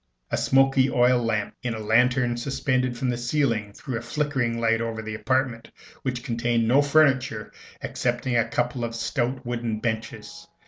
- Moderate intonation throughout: No, narrow, 2.0 semitones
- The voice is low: Yes, low, 120 Hz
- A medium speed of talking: Yes, average, 165 wpm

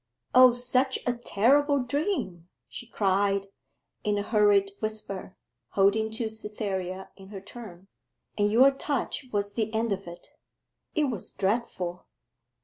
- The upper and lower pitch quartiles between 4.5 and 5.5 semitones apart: No, average, 3.8 semitones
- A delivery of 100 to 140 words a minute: Yes, slow, 135 wpm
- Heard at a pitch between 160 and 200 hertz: No, high, 210 Hz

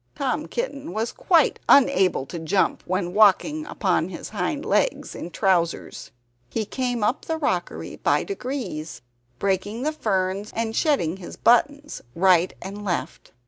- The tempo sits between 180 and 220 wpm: No, average, 140 wpm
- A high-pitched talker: Yes, high, 210 Hz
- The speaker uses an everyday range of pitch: No, wide, 7.1 semitones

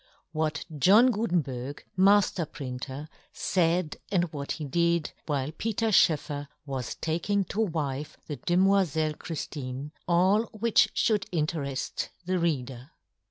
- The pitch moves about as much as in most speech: Yes, average, 4.8 semitones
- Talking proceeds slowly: Yes, slow, 110 wpm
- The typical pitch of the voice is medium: Yes, medium, 160 Hz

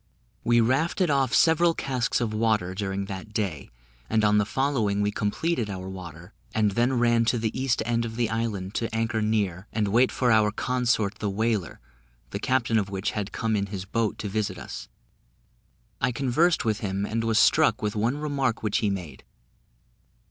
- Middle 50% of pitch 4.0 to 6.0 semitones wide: No, average, 3.0 semitones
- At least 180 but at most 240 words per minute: Yes, average, 185 wpm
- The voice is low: Yes, low, 110 Hz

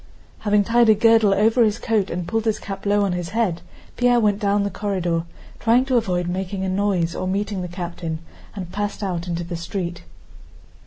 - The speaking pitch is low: No, high, 200 Hz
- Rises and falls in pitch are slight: No, average, 3.2 semitones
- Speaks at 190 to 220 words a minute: Yes, average, 200 wpm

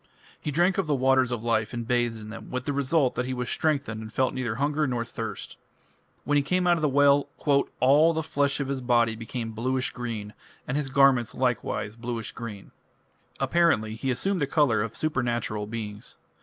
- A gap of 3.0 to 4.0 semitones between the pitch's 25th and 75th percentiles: Yes, average, 3.7 semitones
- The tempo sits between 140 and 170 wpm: No, average, 195 wpm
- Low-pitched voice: Yes, low, 130 Hz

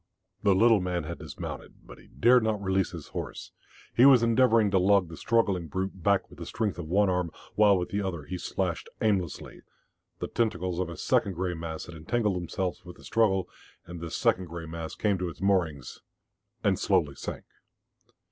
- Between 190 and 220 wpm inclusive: Yes, average, 195 wpm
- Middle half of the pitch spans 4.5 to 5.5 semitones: No, average, 3.2 semitones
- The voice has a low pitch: Yes, very low, 95 Hz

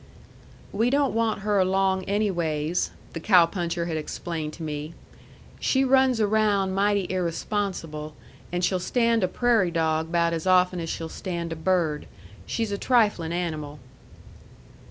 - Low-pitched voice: No, medium, 180 Hz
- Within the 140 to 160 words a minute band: Yes, average, 145 wpm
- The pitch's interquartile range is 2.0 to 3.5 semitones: No, average, 3.9 semitones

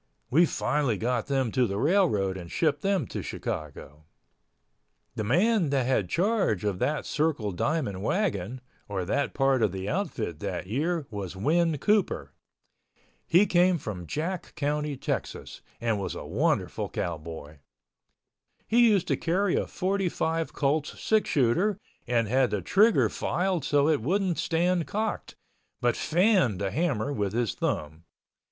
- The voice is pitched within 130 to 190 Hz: Yes, medium, 140 Hz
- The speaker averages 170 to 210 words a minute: No, average, 145 wpm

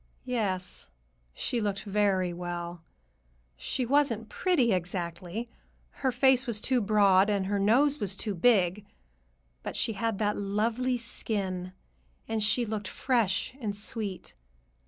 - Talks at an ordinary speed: No, slow, 125 wpm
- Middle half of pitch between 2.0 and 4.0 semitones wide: Yes, average, 3.7 semitones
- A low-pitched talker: No, high, 210 Hz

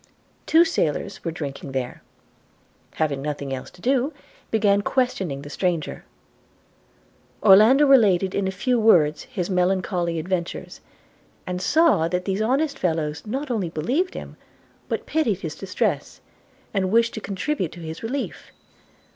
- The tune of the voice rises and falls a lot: Yes, wide, 6.6 semitones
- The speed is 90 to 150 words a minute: Yes, average, 140 wpm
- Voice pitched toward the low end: No, high, 190 Hz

